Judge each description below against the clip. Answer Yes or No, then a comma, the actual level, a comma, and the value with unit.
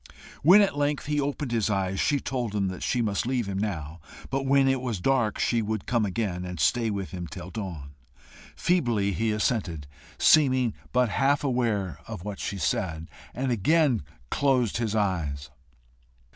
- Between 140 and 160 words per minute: No, average, 170 wpm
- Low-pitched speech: Yes, low, 110 Hz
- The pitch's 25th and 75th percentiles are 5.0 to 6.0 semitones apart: Yes, wide, 5.6 semitones